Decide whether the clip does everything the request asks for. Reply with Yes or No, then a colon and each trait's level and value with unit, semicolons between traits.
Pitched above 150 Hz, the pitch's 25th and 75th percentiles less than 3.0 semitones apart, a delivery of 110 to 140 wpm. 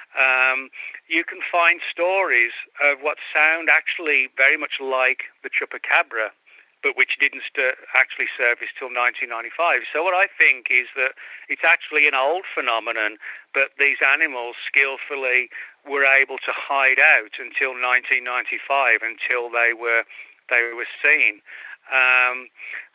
No: low, 130 Hz; narrow, 2.4 semitones; slow, 135 wpm